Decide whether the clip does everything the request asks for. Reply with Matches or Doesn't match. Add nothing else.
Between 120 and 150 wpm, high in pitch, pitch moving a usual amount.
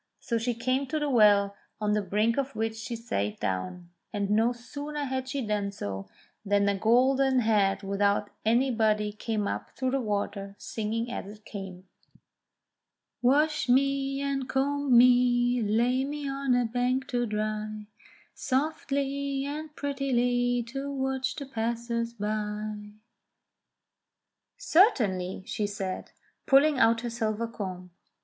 Matches